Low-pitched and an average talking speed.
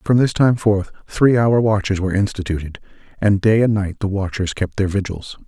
Yes: low, 100 Hz; average, 195 wpm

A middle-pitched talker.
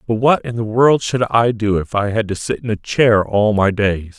No: low, 110 Hz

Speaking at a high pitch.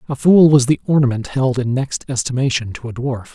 No: low, 130 Hz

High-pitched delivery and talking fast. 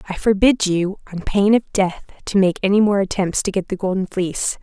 Yes: high, 195 Hz; fast, 220 wpm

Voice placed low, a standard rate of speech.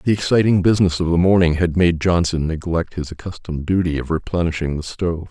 Yes: very low, 85 Hz; average, 190 wpm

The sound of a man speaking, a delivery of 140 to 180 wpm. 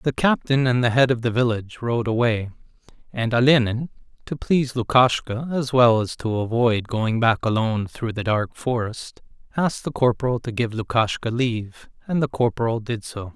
Yes: male; average, 175 wpm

